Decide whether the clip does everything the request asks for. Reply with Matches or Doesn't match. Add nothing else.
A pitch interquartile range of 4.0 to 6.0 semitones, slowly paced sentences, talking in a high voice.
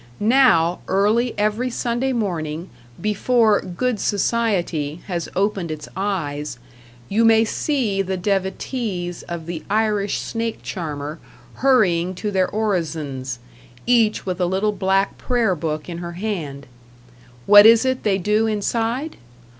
Matches